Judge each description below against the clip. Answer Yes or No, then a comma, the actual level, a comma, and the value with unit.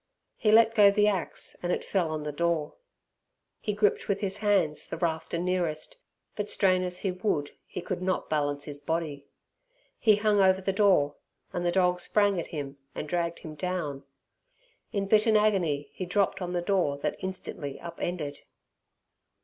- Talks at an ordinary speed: Yes, average, 175 wpm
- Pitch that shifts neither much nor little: Yes, average, 4.4 semitones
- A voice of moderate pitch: Yes, medium, 180 Hz